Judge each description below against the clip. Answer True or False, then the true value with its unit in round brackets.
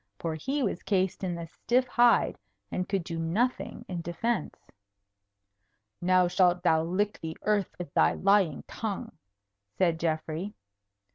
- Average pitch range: True (3.8 semitones)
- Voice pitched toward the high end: False (180 Hz)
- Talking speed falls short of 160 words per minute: True (140 wpm)